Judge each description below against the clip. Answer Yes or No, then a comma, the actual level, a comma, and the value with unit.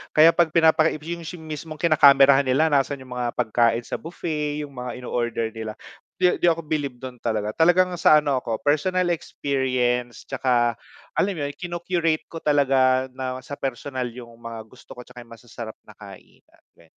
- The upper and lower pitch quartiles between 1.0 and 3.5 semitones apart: No, average, 4.3 semitones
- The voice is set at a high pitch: No, low, 135 Hz